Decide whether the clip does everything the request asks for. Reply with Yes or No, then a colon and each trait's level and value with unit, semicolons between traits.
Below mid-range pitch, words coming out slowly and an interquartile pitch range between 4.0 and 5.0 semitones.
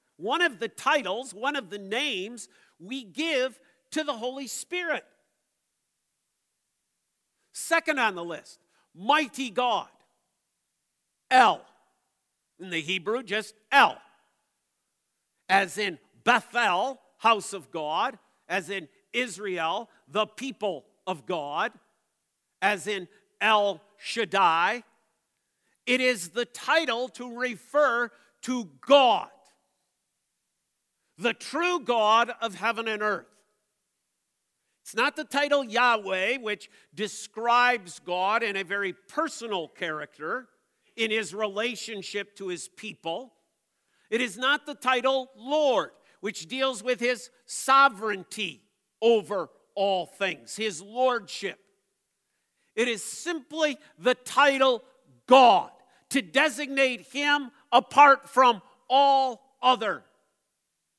No: high, 230 Hz; slow, 105 wpm; average, 4.6 semitones